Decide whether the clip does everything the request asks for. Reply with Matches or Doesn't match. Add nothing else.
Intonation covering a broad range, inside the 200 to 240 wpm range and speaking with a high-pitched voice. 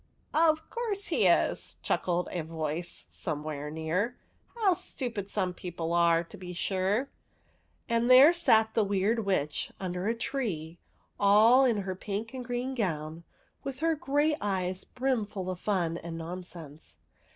Doesn't match